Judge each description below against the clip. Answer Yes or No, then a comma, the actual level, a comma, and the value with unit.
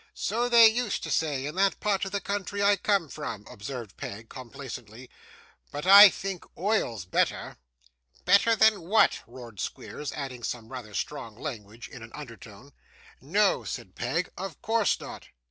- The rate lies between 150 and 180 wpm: Yes, average, 160 wpm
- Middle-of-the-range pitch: Yes, medium, 150 Hz